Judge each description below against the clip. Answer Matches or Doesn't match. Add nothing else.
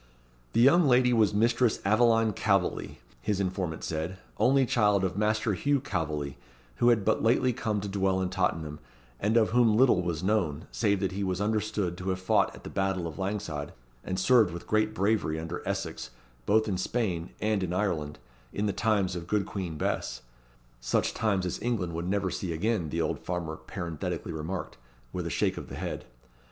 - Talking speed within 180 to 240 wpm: Matches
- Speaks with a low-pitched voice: Matches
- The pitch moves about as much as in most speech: Matches